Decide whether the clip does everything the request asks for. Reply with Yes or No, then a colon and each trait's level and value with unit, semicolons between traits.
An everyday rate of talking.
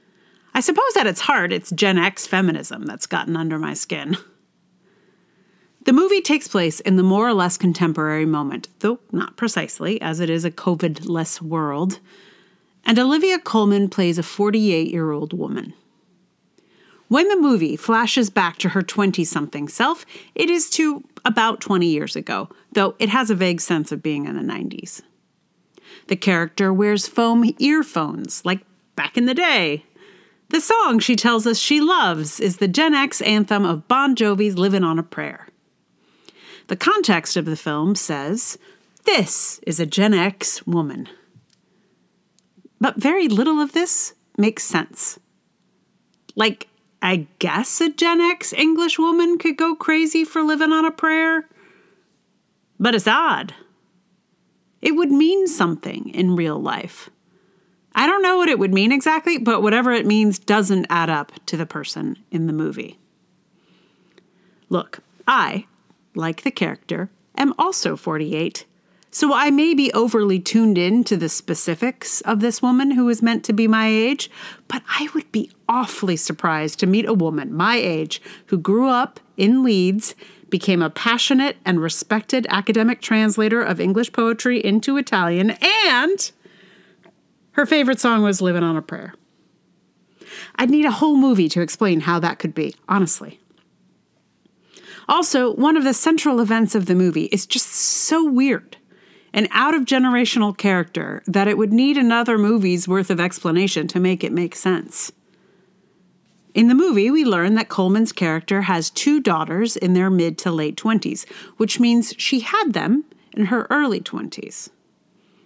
Yes: average, 155 wpm